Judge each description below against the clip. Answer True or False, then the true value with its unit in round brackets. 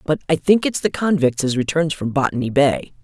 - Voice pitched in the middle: True (150 Hz)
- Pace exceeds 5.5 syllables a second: False (5.4 syllables/s)